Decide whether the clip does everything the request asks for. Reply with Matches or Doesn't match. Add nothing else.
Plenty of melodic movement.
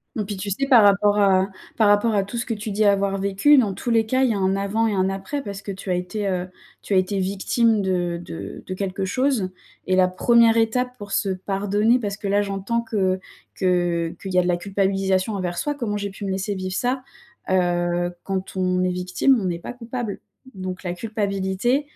Doesn't match